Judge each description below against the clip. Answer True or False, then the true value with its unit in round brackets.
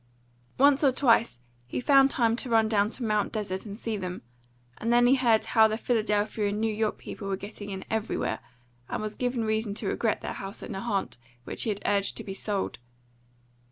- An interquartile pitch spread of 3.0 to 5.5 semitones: False (2.5 semitones)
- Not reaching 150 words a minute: False (205 wpm)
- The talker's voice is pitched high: True (220 Hz)